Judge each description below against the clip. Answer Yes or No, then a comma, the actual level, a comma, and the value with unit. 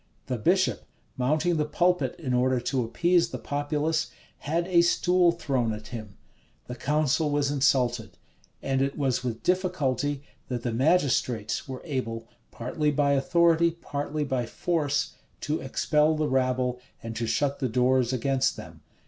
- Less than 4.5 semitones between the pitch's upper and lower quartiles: Yes, average, 4.0 semitones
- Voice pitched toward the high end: No, medium, 140 Hz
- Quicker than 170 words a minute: No, average, 150 wpm